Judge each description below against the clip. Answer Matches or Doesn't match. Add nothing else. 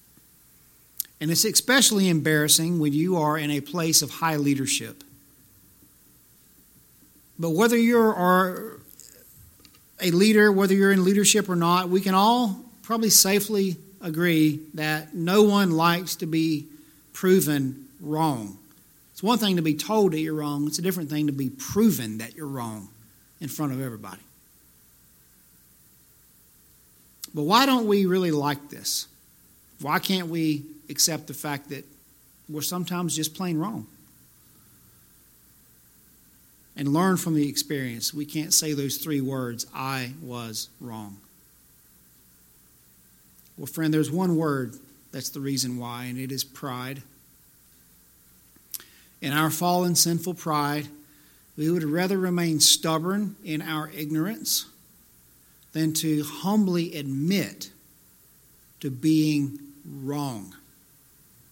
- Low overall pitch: Doesn't match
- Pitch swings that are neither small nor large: Matches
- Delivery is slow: Matches